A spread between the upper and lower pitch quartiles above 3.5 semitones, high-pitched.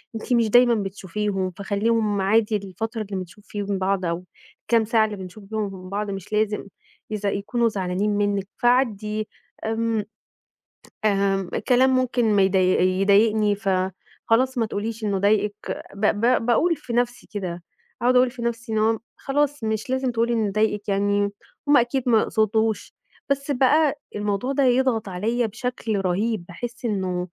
No: average, 3.1 semitones; high, 215 Hz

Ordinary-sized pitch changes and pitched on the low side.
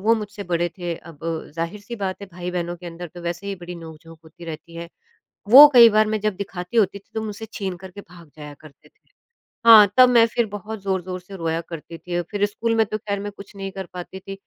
No: average, 3.3 semitones; high, 190 Hz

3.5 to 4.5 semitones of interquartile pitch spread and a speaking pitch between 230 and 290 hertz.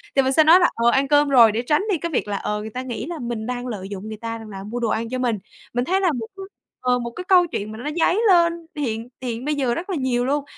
No: average, 4.9 semitones; very high, 250 Hz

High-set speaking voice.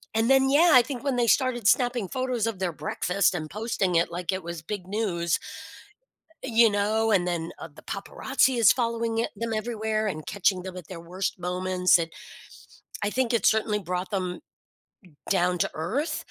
Yes: high, 205 Hz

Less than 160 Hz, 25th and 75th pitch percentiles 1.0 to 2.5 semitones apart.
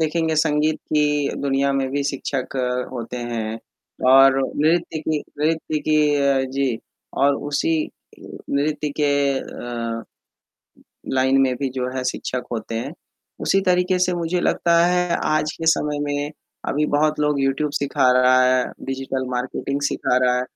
No: medium, 140 Hz; average, 2.9 semitones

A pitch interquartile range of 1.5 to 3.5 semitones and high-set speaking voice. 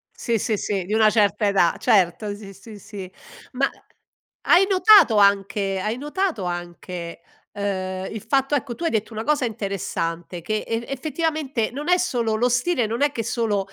No: average, 5.1 semitones; high, 220 Hz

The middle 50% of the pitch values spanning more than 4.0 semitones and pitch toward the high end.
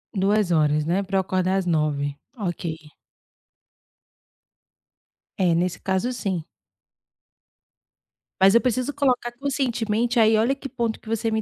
Yes: average, 5.1 semitones; high, 205 Hz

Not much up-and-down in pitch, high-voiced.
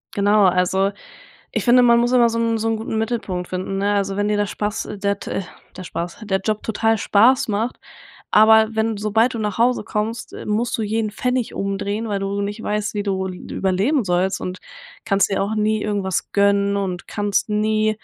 Yes: narrow, 2.1 semitones; high, 210 Hz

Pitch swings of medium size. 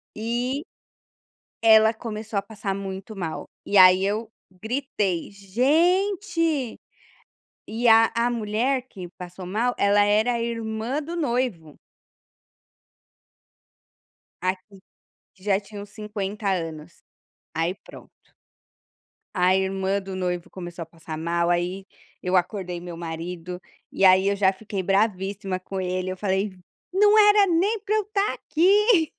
Yes: average, 4.7 semitones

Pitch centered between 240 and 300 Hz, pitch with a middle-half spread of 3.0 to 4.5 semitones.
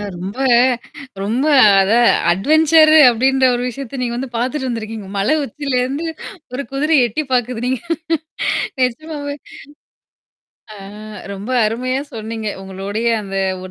Yes: very high, 250 Hz; average, 4.1 semitones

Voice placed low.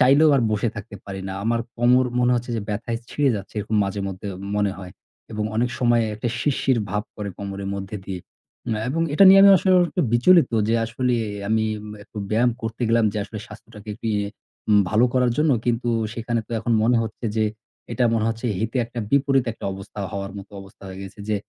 Yes: low, 115 Hz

